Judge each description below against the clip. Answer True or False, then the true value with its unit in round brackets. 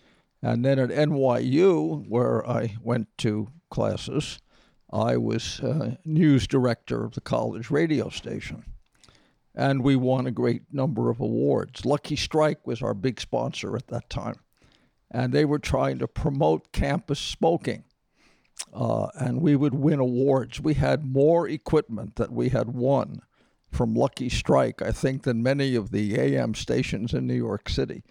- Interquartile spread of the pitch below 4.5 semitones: True (3.8 semitones)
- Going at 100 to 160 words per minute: True (155 wpm)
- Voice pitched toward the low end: True (130 Hz)